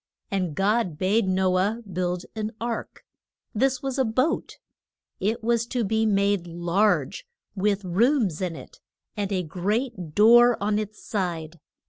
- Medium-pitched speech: No, high, 205 Hz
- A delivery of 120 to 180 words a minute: Yes, average, 145 wpm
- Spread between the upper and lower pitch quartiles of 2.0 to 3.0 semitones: No, average, 3.8 semitones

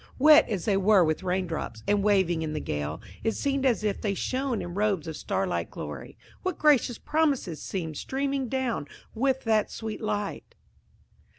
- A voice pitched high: Yes, high, 210 Hz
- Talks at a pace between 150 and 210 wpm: Yes, average, 175 wpm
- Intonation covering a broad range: Yes, wide, 6.5 semitones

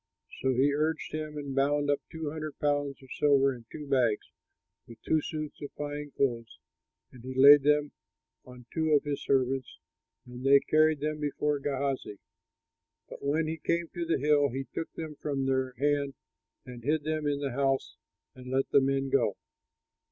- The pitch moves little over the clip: Yes, narrow, 2.0 semitones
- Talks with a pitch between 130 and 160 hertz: Yes, medium, 140 Hz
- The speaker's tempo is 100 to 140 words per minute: No, average, 175 wpm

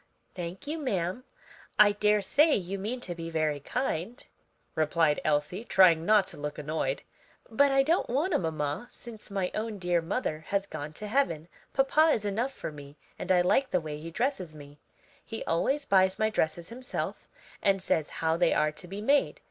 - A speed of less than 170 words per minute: No, average, 185 wpm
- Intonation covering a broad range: Yes, wide, 6.6 semitones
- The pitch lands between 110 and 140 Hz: No, high, 190 Hz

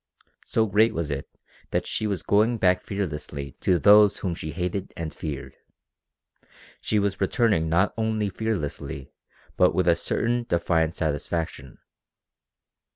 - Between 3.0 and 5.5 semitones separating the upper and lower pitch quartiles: Yes, average, 4.6 semitones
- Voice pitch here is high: No, very low, 90 Hz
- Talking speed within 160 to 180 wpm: No, slow, 135 wpm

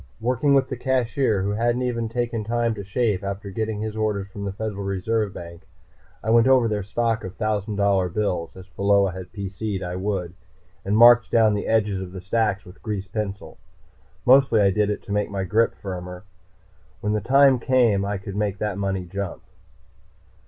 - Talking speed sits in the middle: Yes, average, 190 wpm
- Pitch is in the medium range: No, low, 105 Hz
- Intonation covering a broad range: No, average, 2.7 semitones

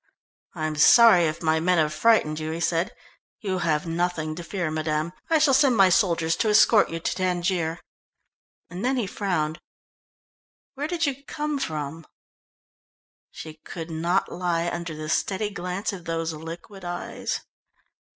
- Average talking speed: Yes, average, 160 wpm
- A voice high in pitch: No, medium, 175 Hz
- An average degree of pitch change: Yes, average, 3.7 semitones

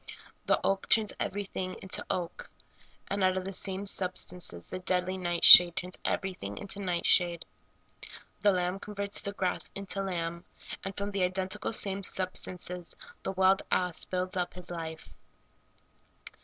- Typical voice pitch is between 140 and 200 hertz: Yes, medium, 185 Hz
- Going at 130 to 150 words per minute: Yes, average, 145 wpm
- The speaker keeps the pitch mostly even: Yes, narrow, 1.5 semitones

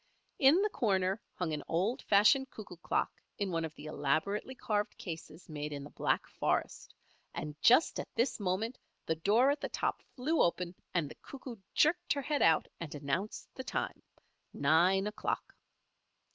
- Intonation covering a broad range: Yes, wide, 7.5 semitones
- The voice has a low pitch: No, high, 195 Hz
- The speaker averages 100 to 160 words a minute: No, average, 170 wpm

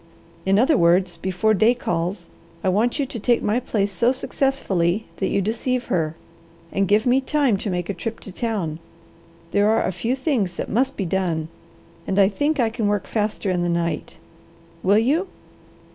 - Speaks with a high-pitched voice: Yes, high, 205 Hz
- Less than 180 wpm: No, average, 190 wpm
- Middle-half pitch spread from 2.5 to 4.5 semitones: No, average, 4.9 semitones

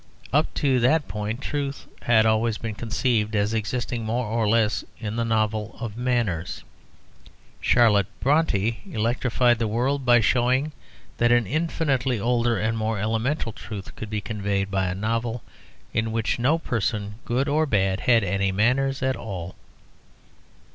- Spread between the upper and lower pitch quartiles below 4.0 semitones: Yes, average, 2.9 semitones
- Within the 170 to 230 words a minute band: No, average, 150 wpm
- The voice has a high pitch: No, low, 115 Hz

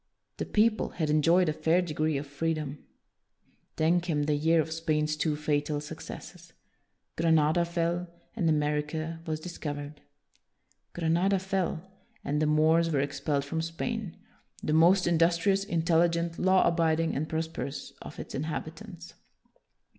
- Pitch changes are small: Yes, narrow, 2.0 semitones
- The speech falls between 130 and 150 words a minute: Yes, average, 140 wpm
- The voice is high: No, medium, 160 Hz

